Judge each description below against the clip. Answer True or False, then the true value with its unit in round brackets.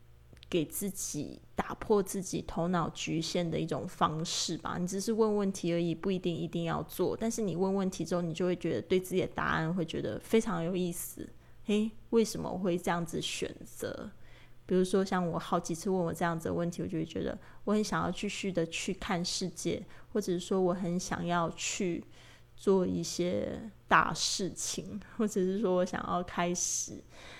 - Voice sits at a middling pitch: True (180 Hz)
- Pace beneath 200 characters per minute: False (275 characters per minute)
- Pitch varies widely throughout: False (2.5 semitones)